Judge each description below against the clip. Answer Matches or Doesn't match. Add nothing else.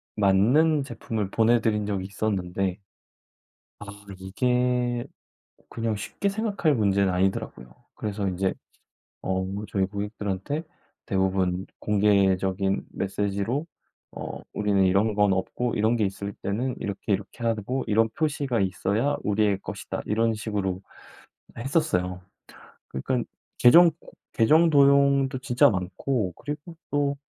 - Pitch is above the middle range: Doesn't match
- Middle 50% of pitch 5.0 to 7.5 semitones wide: Doesn't match